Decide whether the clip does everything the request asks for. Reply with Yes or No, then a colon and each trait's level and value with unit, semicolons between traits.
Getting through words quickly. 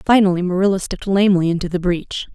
No: average, 180 wpm